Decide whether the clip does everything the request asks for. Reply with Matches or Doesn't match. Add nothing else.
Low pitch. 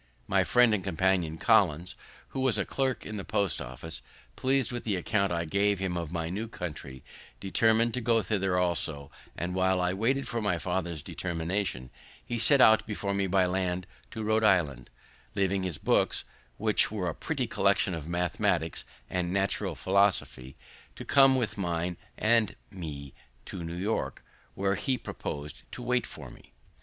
Matches